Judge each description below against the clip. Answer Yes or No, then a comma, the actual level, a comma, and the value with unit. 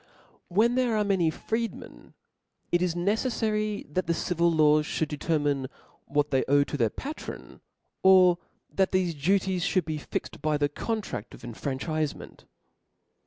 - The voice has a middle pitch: Yes, medium, 170 Hz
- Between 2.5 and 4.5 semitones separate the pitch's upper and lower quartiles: No, average, 5.0 semitones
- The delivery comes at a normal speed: Yes, average, 145 wpm